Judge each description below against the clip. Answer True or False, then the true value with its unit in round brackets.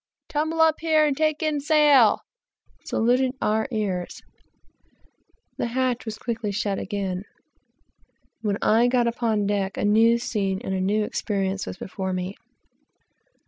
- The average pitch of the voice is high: True (220 Hz)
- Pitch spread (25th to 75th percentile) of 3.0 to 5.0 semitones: True (4.7 semitones)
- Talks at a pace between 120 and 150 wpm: True (140 wpm)